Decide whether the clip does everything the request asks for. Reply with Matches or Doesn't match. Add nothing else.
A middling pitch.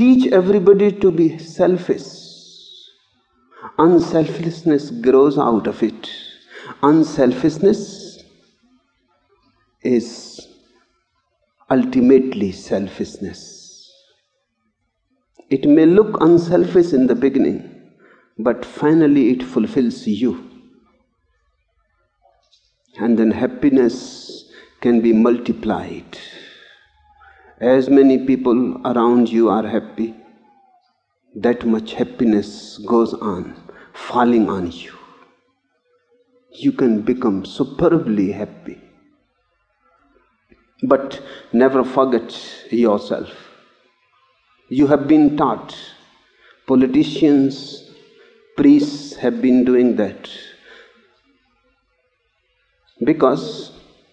Matches